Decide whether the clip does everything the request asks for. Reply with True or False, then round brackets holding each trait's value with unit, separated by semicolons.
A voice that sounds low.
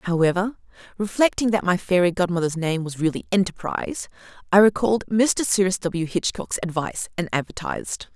False (185 Hz)